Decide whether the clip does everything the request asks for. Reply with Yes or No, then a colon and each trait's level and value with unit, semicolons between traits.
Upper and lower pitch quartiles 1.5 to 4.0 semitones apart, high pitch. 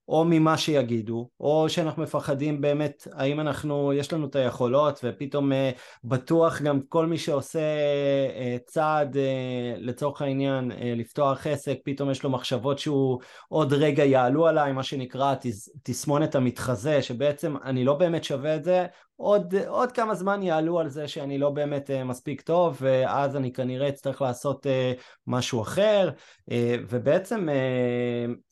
No: average, 2.9 semitones; medium, 140 Hz